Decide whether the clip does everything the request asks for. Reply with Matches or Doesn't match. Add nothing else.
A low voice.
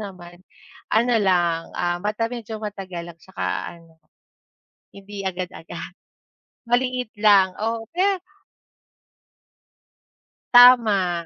Doesn't match